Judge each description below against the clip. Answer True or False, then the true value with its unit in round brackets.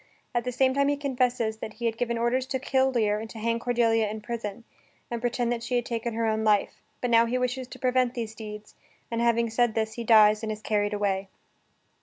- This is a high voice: True (230 Hz)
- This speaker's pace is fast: True (235 wpm)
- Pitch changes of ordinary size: False (2.2 semitones)